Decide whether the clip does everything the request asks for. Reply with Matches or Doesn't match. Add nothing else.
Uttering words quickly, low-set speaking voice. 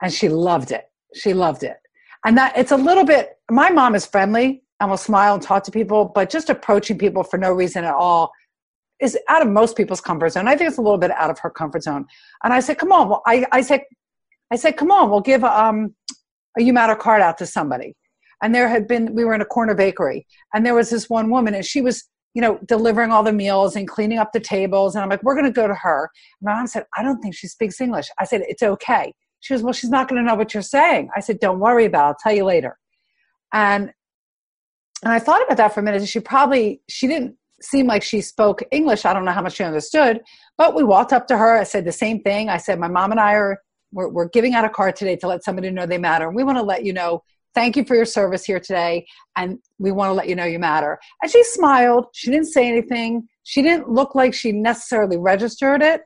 Doesn't match